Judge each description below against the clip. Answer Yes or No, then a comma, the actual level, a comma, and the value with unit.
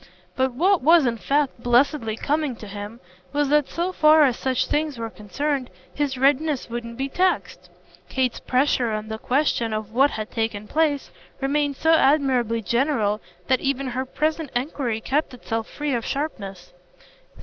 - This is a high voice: Yes, very high, 265 Hz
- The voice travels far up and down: No, average, 4.2 semitones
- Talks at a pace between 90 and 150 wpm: No, average, 160 wpm